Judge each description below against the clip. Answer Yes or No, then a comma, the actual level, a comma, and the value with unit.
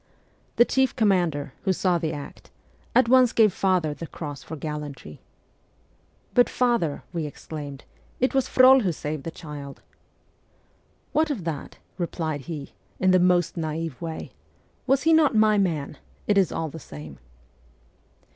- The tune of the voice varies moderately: No, wide, 6.4 semitones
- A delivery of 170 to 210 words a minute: Yes, average, 175 wpm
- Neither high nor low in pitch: Yes, medium, 170 Hz